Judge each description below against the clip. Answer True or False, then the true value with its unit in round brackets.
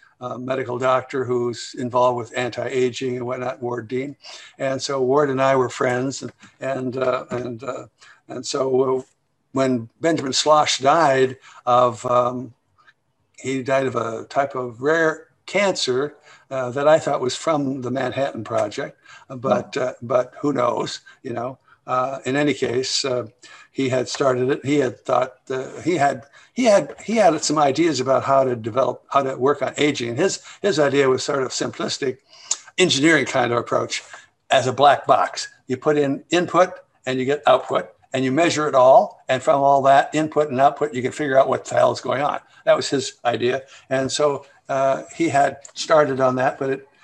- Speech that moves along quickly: False (180 wpm)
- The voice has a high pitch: False (135 Hz)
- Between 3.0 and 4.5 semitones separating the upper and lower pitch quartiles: False (2.5 semitones)